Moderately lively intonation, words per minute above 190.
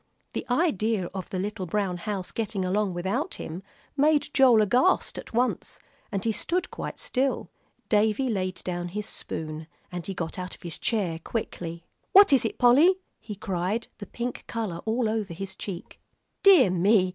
No: average, 4.8 semitones; average, 170 wpm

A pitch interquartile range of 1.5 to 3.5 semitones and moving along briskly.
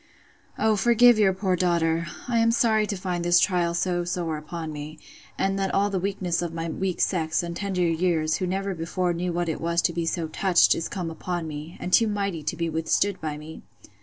Yes: average, 2.8 semitones; fast, 215 wpm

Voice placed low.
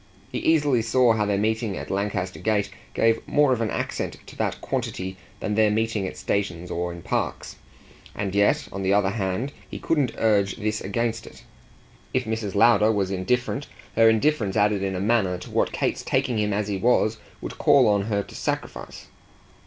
Yes: low, 105 Hz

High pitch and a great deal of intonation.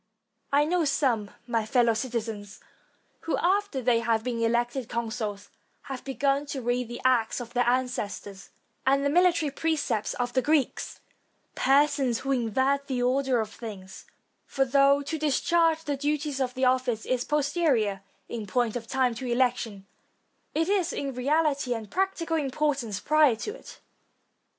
No: very high, 255 Hz; average, 3.7 semitones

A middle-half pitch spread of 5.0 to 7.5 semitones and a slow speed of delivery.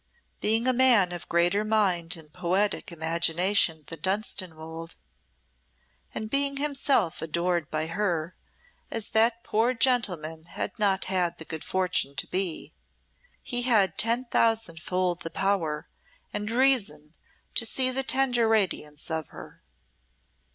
Yes: wide, 5.6 semitones; slow, 130 wpm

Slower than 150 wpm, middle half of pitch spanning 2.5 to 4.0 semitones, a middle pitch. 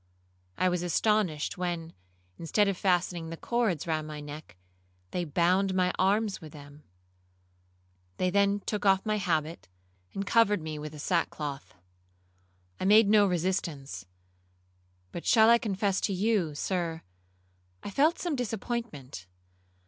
No: slow, 135 wpm; average, 4.6 semitones; medium, 180 Hz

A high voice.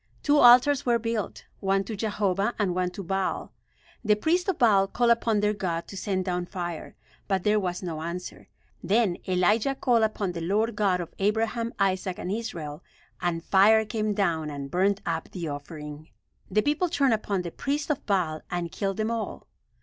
Yes: high, 195 Hz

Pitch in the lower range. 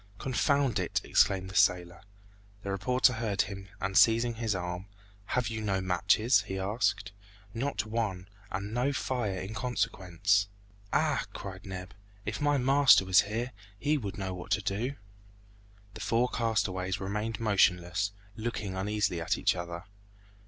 Yes: low, 105 Hz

